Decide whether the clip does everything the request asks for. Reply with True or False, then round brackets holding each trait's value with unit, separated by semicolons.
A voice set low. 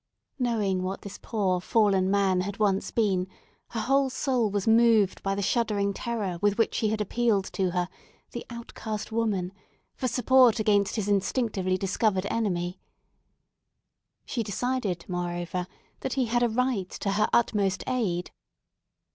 False (205 Hz)